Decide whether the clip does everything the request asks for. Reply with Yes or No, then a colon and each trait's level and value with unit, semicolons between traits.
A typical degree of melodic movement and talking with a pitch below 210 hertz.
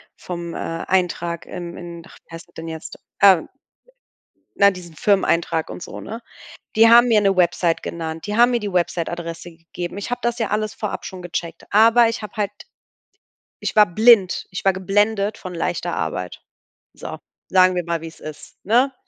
Yes: average, 3.9 semitones; medium, 185 Hz